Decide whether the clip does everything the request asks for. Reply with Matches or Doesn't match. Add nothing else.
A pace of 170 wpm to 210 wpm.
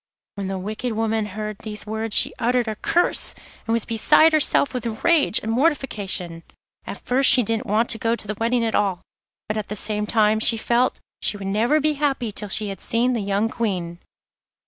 Matches